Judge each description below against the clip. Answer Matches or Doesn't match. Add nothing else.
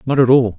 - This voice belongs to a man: Matches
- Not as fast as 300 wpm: Doesn't match